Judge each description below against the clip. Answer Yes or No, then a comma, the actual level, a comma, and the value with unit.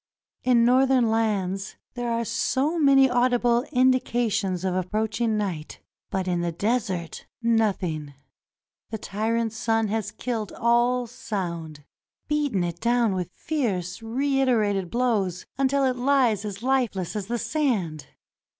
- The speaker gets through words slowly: Yes, slow, 130 wpm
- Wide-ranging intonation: No, average, 4.6 semitones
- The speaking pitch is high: Yes, high, 225 Hz